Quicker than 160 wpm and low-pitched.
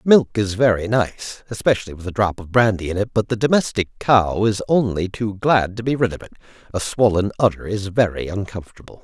Yes: fast, 205 wpm; low, 105 Hz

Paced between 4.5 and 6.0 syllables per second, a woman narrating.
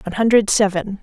No: 6.6 syllables/s; female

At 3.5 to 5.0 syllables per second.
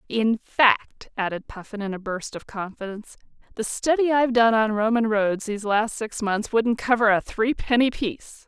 Yes: 4.9 syllables/s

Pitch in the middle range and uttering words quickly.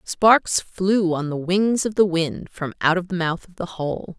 Yes: medium, 180 Hz; fast, 230 wpm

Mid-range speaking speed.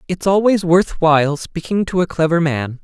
Yes: average, 190 wpm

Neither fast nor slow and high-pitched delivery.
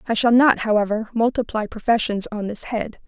Yes: average, 175 wpm; high, 220 Hz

